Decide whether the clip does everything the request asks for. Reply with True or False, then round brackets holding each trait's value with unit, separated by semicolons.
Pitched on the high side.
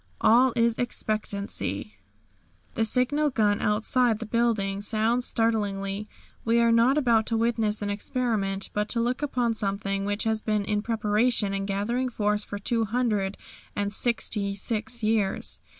True (220 Hz)